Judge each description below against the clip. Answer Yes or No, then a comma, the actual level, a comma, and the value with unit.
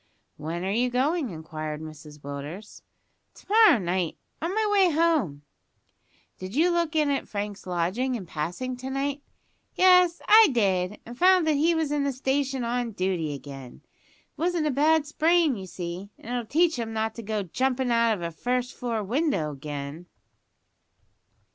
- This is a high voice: Yes, high, 240 Hz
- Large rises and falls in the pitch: Yes, wide, 9.0 semitones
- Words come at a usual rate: Yes, average, 170 wpm